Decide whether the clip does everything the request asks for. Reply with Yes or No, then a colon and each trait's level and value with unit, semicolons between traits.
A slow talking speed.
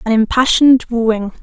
Yes: slow, 125 wpm